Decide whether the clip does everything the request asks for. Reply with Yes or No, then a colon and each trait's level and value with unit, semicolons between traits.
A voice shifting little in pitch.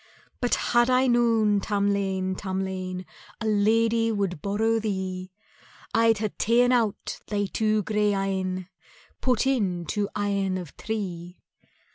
No: average, 3.0 semitones